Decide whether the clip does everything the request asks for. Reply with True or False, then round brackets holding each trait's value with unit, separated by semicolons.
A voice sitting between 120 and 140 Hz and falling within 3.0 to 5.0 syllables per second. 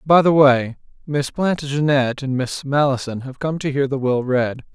True (135 Hz; 4.7 syllables/s)